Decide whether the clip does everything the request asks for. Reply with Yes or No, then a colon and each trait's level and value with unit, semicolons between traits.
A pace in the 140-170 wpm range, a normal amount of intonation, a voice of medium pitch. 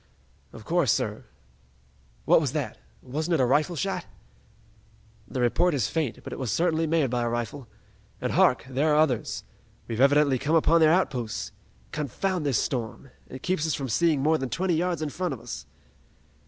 No: average, 180 wpm; average, 4.1 semitones; medium, 145 Hz